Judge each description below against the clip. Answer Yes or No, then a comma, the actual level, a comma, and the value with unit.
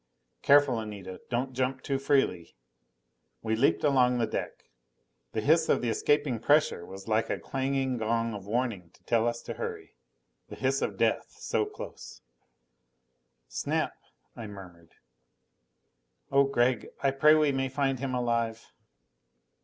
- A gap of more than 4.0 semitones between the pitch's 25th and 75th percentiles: No, average, 3.7 semitones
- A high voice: No, low, 125 Hz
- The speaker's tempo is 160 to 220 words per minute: No, average, 145 wpm